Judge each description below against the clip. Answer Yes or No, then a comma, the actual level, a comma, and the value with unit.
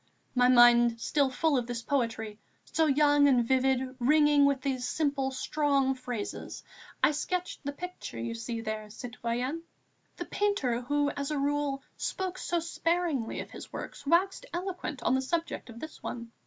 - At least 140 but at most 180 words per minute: Yes, average, 165 wpm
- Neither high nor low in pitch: No, very high, 275 Hz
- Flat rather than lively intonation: No, average, 3.8 semitones